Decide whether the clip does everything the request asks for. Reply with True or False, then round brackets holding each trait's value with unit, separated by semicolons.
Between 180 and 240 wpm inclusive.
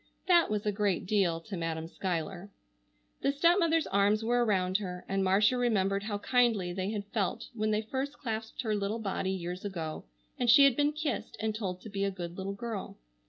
True (200 wpm)